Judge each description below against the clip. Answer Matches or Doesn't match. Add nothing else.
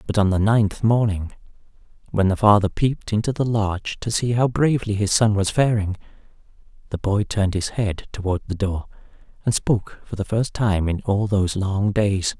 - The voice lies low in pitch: Matches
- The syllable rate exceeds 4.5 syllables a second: Matches